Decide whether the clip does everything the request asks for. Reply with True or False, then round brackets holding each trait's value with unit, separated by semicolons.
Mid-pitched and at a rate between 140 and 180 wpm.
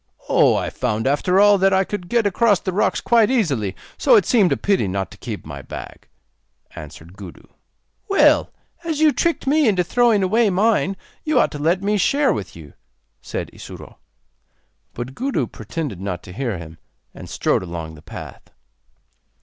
True (180 Hz; 175 wpm)